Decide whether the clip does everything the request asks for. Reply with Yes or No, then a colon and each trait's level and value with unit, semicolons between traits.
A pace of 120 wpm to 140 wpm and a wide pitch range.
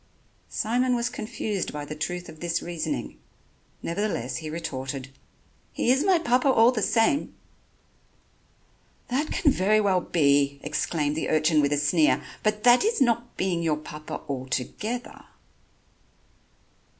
Yes: slow, 135 wpm; wide, 8.0 semitones